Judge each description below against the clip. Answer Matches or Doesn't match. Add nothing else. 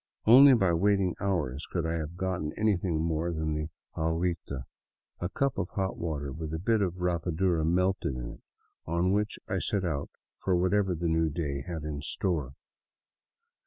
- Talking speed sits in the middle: Matches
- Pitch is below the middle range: Matches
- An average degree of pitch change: Matches